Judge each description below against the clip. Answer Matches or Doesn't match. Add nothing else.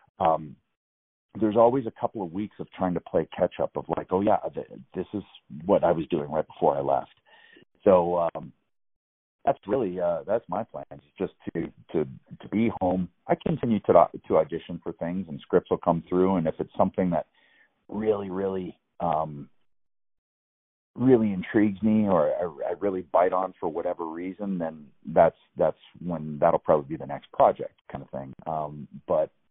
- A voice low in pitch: Matches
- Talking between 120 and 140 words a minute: Doesn't match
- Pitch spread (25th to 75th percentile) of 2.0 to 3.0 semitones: Doesn't match